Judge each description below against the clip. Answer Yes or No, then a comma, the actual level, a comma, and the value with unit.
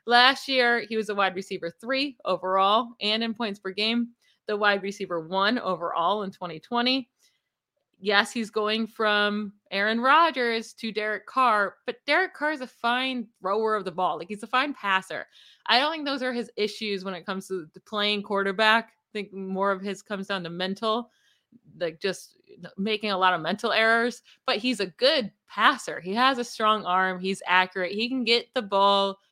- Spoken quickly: No, average, 190 wpm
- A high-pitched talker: Yes, high, 210 Hz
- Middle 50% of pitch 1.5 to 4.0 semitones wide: Yes, average, 3.7 semitones